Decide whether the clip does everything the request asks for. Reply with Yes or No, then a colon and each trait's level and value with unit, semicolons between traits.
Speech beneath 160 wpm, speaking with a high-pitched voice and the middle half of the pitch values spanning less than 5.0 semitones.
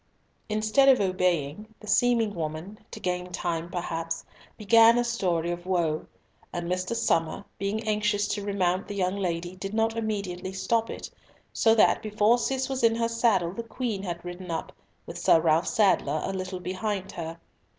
No: average, 170 wpm; high, 195 Hz; average, 4.0 semitones